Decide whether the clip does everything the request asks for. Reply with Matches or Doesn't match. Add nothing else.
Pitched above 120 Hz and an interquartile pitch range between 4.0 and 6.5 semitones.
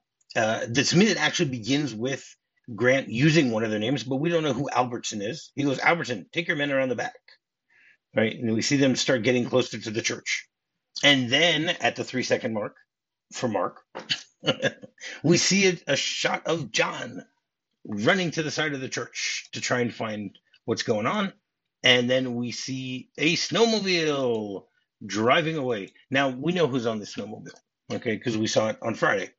Matches